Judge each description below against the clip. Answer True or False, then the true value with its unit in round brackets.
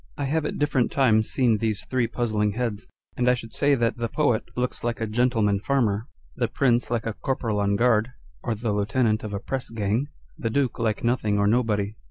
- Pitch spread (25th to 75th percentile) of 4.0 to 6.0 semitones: False (2.7 semitones)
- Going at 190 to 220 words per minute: True (205 wpm)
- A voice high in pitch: False (115 Hz)